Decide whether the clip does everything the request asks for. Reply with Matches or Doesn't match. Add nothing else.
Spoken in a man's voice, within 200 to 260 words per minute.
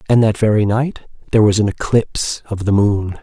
Matches